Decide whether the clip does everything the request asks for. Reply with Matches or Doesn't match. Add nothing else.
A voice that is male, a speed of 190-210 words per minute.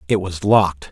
Matches